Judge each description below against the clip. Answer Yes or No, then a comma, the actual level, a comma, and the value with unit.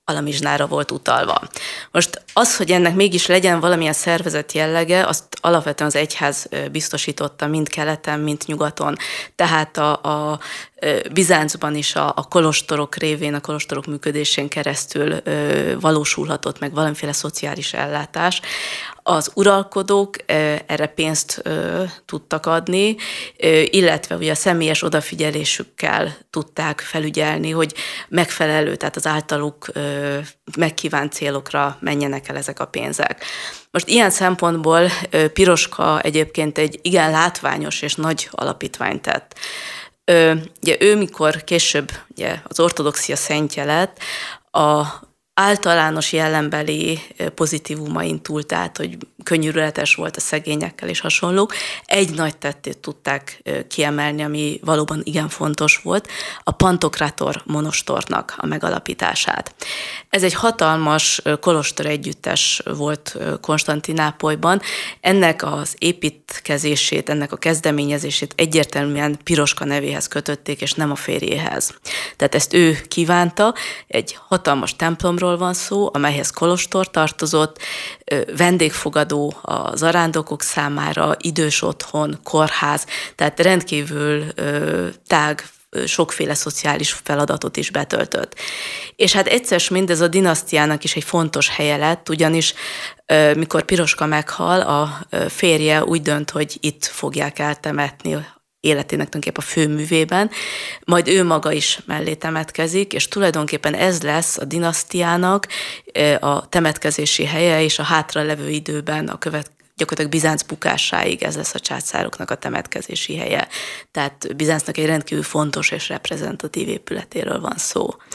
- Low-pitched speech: No, medium, 155 Hz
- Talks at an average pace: Yes, average, 120 wpm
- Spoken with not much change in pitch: Yes, narrow, 2.1 semitones